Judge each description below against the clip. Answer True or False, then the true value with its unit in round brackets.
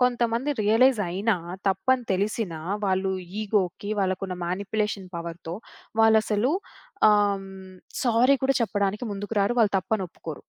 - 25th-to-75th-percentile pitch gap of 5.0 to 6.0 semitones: False (3.0 semitones)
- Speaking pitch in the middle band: False (205 Hz)